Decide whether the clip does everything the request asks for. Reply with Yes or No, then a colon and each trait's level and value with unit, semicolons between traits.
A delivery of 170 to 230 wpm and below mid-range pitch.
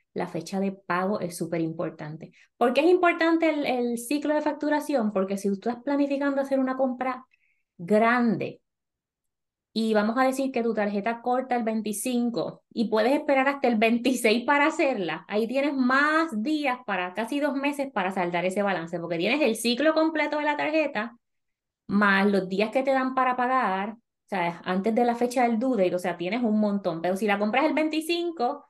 No: fast, 190 wpm; high, 235 Hz